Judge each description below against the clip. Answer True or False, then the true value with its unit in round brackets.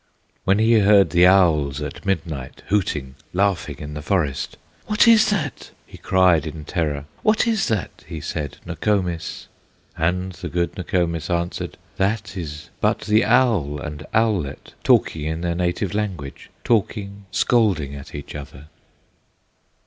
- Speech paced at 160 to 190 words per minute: False (140 wpm)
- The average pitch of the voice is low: True (90 Hz)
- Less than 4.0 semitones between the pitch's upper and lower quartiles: False (5.3 semitones)